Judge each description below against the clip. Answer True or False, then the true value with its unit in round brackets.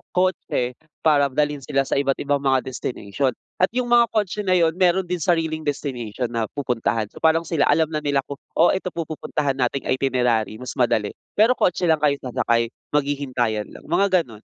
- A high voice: False (145 Hz)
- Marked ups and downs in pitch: False (4.8 semitones)